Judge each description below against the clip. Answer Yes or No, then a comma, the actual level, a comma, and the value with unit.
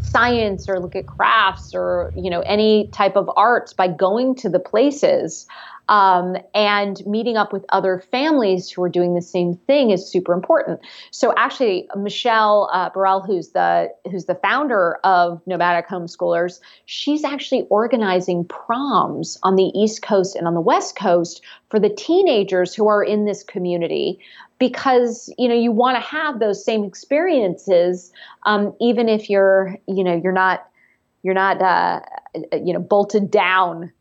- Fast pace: No, average, 160 wpm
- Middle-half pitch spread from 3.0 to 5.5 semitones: Yes, average, 3.4 semitones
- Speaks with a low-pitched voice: No, high, 195 Hz